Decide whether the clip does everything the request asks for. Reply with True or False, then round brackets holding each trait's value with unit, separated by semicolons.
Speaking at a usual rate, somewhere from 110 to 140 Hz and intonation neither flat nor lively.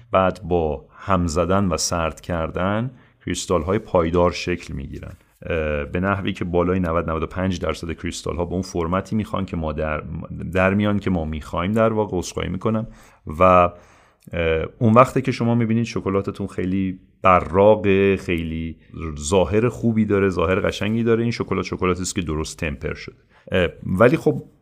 False (155 wpm; 95 Hz; 3.6 semitones)